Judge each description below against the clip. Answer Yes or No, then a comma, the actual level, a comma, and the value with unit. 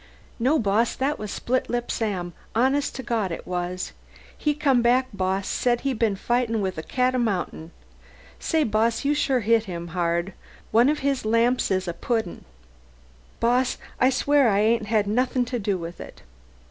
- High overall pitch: Yes, high, 230 Hz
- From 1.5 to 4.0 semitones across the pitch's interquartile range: No, average, 4.5 semitones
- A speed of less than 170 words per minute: No, average, 175 wpm